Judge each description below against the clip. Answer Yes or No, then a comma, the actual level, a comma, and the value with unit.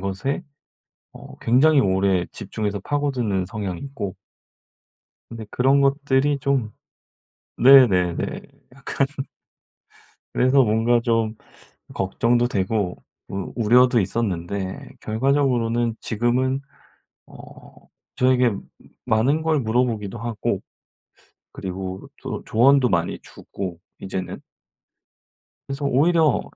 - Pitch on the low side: Yes, low, 115 Hz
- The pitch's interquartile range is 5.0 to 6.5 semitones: Yes, average, 5.3 semitones